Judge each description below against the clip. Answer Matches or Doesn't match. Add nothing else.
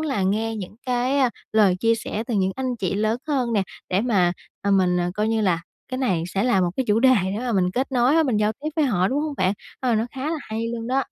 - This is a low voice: Doesn't match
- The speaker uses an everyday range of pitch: Matches